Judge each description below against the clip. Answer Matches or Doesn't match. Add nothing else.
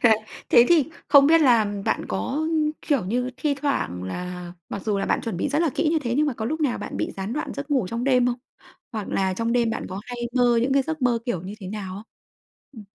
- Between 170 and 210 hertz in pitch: Doesn't match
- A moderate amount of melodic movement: Doesn't match